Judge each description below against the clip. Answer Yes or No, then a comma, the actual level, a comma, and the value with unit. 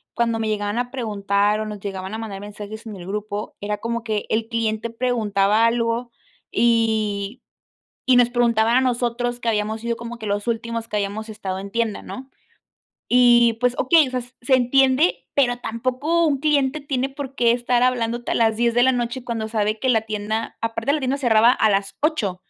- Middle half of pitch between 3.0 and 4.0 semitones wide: No, narrow, 2.5 semitones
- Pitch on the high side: Yes, high, 230 Hz